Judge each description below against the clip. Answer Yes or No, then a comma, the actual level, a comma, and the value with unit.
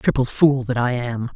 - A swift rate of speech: Yes, fast, 220 wpm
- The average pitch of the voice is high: No, low, 125 Hz